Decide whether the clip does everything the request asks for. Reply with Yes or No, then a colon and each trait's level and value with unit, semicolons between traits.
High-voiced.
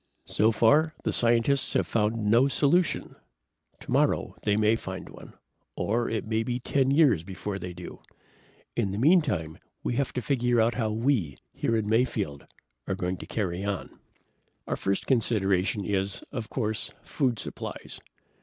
No: low, 110 Hz